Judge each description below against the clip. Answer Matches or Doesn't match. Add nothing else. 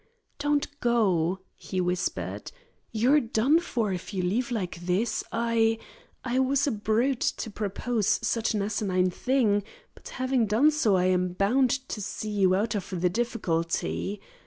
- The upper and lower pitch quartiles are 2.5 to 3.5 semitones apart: Doesn't match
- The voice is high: Matches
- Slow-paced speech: Doesn't match